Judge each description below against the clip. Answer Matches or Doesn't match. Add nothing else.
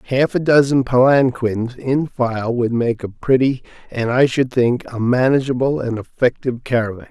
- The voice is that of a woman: Doesn't match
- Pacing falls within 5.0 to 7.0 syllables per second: Doesn't match